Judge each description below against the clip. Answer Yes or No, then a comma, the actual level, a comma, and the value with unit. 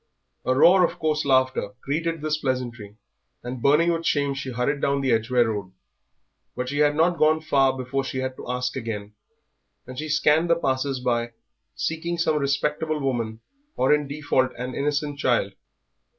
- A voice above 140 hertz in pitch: No, low, 135 Hz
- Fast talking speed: No, average, 170 wpm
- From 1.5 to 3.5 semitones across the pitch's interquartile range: Yes, average, 3.2 semitones